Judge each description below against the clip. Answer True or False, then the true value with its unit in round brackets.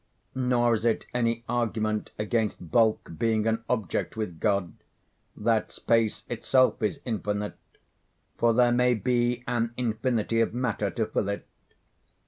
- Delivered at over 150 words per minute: False (135 wpm)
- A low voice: True (115 Hz)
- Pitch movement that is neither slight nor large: False (2.1 semitones)